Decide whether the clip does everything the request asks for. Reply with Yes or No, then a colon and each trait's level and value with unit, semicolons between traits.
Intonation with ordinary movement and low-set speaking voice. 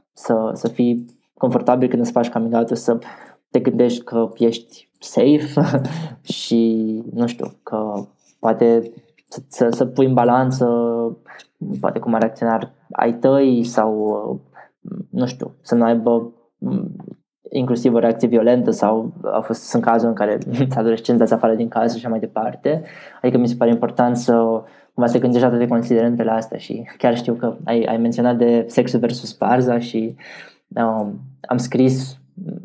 No: narrow, 1.2 semitones; low, 120 Hz